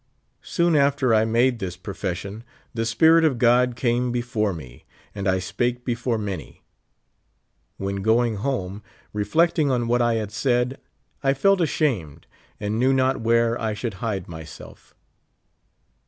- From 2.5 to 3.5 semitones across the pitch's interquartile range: No, average, 4.0 semitones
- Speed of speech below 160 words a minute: Yes, average, 140 wpm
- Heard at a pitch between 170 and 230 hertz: No, low, 115 Hz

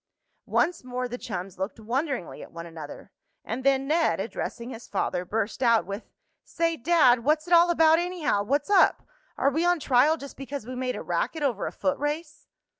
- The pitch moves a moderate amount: No, wide, 5.7 semitones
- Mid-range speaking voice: No, very high, 270 Hz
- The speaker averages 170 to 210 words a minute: Yes, average, 190 wpm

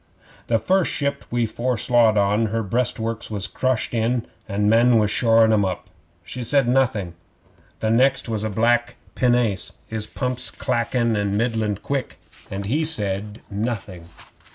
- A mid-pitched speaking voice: No, low, 115 Hz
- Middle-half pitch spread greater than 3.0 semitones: No, average, 2.7 semitones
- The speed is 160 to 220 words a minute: No, average, 145 wpm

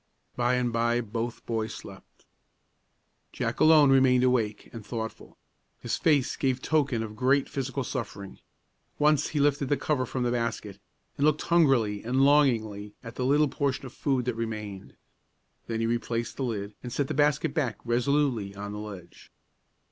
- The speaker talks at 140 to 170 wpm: Yes, average, 165 wpm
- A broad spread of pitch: No, average, 3.8 semitones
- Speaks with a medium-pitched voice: No, low, 125 Hz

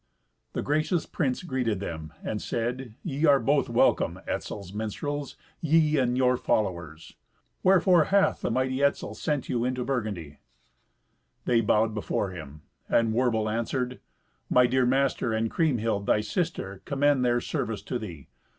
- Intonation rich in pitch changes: No, average, 4.5 semitones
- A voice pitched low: Yes, low, 125 Hz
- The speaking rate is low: No, average, 145 wpm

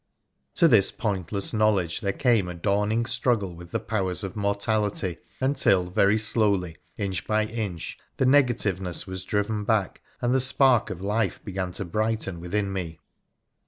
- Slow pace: No, average, 155 wpm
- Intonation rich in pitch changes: No, average, 3.0 semitones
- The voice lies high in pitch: No, low, 100 Hz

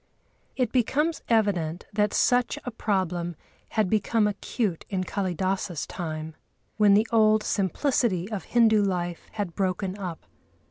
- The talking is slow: Yes, slow, 130 wpm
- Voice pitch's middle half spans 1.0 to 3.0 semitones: No, average, 3.5 semitones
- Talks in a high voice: Yes, high, 200 Hz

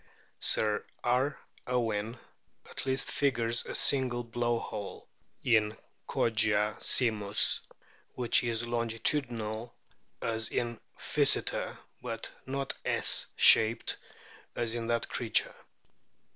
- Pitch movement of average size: No, narrow, 1.7 semitones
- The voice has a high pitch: No, low, 115 Hz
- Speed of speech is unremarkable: No, slow, 100 wpm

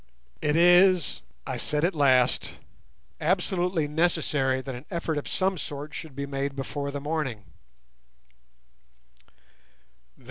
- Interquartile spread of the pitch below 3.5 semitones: No, average, 3.8 semitones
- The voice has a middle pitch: Yes, medium, 150 Hz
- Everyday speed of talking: No, slow, 115 wpm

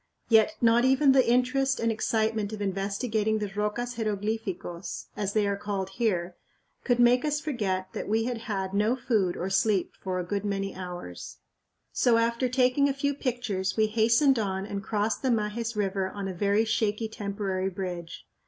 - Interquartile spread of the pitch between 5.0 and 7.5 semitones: No, average, 3.3 semitones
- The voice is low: No, high, 215 Hz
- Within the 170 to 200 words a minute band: Yes, average, 175 wpm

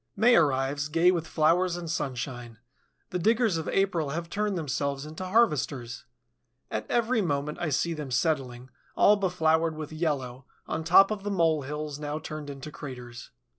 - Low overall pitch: No, medium, 155 Hz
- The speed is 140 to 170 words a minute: Yes, average, 165 wpm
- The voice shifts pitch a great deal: No, average, 4.1 semitones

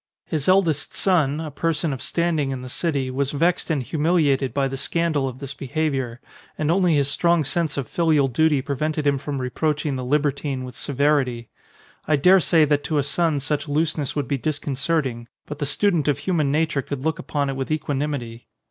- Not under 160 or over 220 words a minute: Yes, average, 195 wpm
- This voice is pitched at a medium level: Yes, medium, 145 Hz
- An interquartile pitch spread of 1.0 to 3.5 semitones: Yes, average, 2.7 semitones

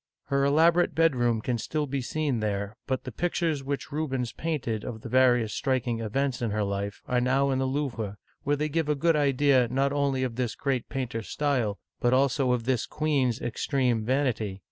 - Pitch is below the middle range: Yes, low, 130 Hz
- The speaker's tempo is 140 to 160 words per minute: No, average, 190 wpm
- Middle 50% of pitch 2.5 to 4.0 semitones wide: Yes, average, 3.3 semitones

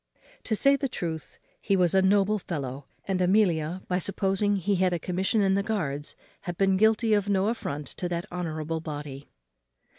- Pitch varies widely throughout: No, average, 3.8 semitones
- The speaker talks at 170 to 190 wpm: Yes, average, 180 wpm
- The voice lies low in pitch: No, medium, 185 Hz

